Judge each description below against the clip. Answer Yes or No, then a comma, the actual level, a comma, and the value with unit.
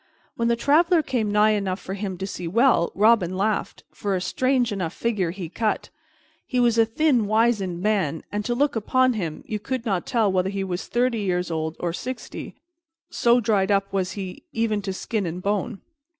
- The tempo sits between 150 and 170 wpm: No, average, 200 wpm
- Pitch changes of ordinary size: Yes, average, 3.9 semitones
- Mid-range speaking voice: No, high, 210 Hz